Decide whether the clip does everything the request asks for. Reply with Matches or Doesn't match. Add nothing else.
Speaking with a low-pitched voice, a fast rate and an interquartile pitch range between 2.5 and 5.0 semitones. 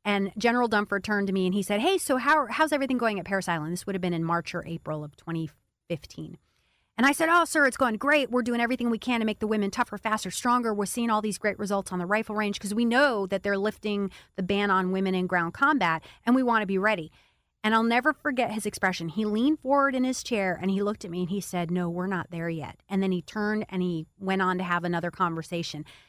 Doesn't match